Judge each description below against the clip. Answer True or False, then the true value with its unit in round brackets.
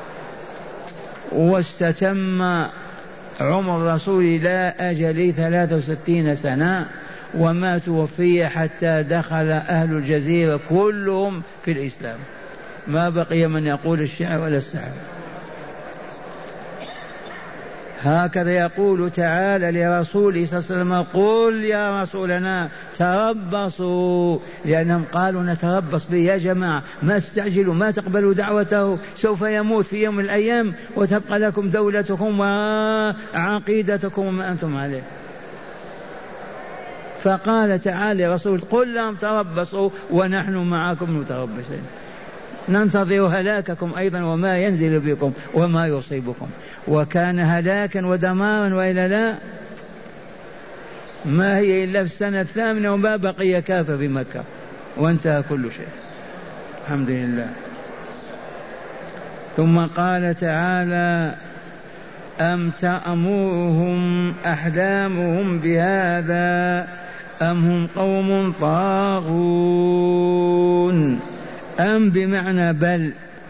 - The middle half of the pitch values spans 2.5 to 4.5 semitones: True (2.8 semitones)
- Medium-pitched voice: True (180 Hz)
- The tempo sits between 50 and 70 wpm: False (90 wpm)